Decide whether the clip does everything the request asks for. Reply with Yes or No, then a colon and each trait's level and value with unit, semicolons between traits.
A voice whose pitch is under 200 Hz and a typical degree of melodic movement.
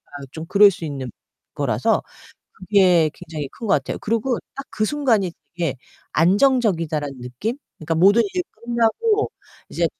No: high, 190 Hz; wide, 6.9 semitones